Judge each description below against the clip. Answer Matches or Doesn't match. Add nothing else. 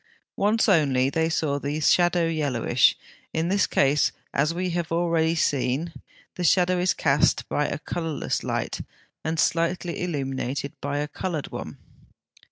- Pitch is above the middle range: Doesn't match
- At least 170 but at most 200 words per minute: Doesn't match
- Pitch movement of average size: Matches